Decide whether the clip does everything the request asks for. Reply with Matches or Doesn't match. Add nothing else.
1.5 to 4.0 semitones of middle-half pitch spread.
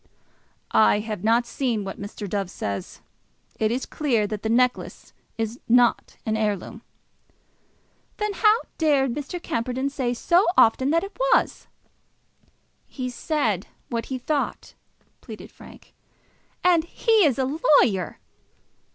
Doesn't match